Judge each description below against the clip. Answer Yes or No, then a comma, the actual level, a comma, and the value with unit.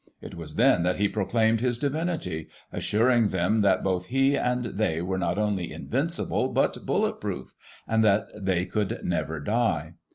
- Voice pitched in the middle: No, low, 105 Hz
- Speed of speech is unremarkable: Yes, average, 170 wpm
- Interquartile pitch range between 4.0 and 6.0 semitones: Yes, average, 4.7 semitones